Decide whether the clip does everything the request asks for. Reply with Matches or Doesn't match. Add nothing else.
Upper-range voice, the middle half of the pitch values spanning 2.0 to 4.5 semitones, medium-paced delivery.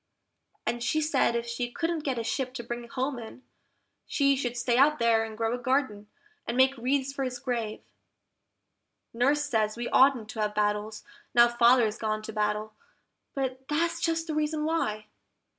Matches